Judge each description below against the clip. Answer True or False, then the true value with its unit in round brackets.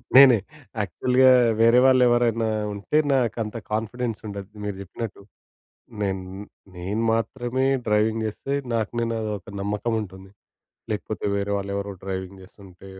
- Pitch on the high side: False (110 Hz)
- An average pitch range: True (3.1 semitones)